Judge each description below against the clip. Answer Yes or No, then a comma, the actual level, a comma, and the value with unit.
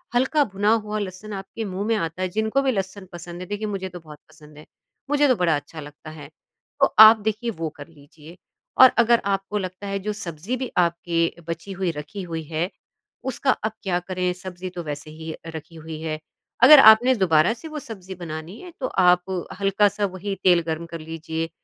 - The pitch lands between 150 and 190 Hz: Yes, medium, 185 Hz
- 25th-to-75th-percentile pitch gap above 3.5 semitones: Yes, average, 4.5 semitones